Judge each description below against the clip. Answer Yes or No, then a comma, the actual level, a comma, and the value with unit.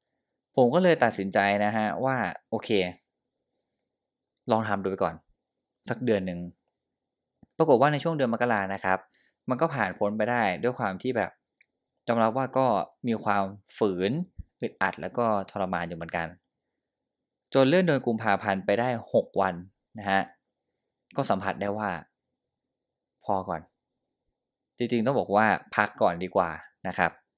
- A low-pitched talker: Yes, low, 105 Hz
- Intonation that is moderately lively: Yes, average, 4.3 semitones